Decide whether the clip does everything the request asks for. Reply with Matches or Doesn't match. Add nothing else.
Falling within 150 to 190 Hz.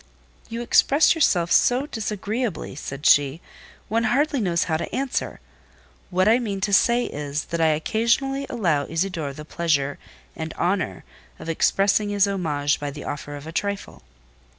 Matches